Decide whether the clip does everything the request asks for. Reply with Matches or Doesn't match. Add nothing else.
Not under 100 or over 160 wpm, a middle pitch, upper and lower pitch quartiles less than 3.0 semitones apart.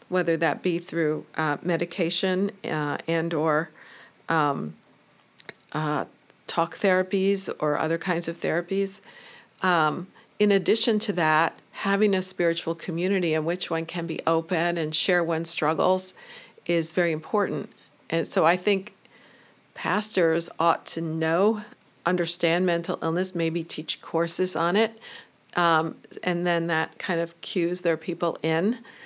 Matches